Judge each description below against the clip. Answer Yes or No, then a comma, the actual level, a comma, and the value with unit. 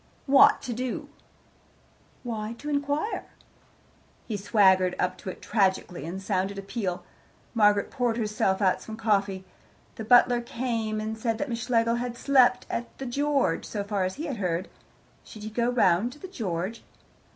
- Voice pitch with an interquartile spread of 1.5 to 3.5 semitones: No, average, 3.9 semitones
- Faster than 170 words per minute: No, average, 165 wpm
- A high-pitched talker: Yes, high, 220 Hz